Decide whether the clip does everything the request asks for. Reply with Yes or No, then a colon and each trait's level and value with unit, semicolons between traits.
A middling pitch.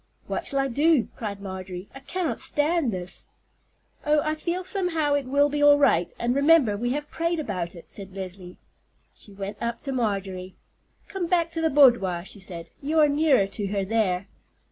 No: high, 245 Hz